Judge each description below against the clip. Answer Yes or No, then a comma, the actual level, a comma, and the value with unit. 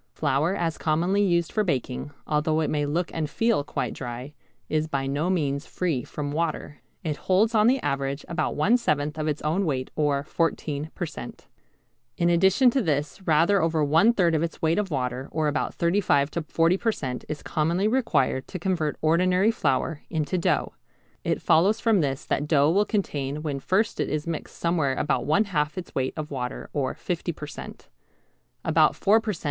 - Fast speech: No, average, 195 wpm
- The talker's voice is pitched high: No, medium, 160 Hz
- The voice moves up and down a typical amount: Yes, average, 4.0 semitones